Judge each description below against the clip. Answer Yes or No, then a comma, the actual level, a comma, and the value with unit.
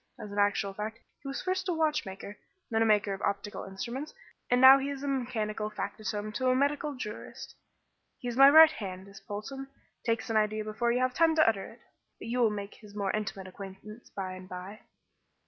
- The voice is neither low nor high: No, high, 215 Hz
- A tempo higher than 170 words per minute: Yes, fast, 205 wpm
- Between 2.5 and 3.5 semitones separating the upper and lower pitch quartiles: No, average, 4.6 semitones